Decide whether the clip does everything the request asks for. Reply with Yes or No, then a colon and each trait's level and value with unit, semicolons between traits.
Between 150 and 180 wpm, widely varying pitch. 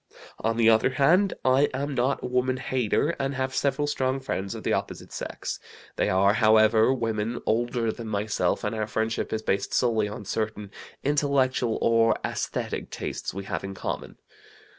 No: average, 170 wpm; average, 3.3 semitones